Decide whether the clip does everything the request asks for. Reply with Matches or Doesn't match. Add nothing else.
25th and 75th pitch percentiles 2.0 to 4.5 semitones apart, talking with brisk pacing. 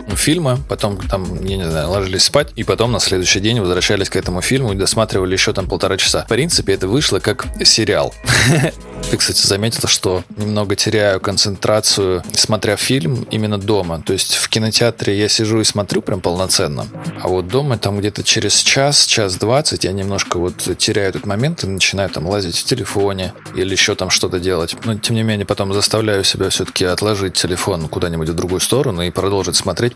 Matches